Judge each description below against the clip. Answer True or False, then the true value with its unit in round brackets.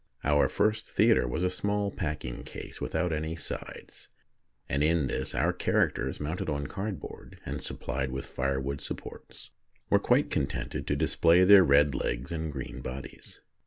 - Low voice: True (75 Hz)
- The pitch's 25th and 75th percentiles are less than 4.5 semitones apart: False (4.8 semitones)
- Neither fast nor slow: True (155 wpm)